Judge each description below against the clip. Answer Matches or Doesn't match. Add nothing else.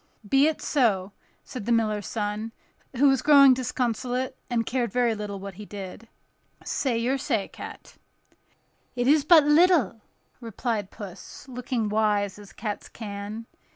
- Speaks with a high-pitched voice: Matches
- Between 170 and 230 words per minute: Doesn't match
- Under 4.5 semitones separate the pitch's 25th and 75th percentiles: Matches